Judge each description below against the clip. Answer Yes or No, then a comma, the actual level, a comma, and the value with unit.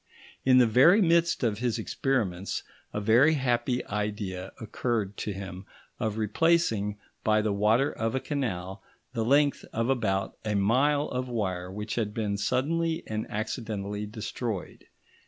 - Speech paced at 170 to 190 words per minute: No, average, 145 wpm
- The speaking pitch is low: Yes, low, 110 Hz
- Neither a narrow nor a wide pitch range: Yes, average, 3.9 semitones